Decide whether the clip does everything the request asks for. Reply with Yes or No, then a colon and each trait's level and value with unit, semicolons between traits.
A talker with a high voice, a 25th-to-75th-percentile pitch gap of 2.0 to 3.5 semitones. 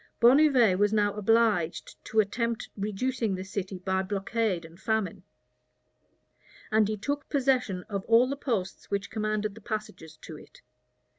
Yes: high, 210 Hz; average, 3.2 semitones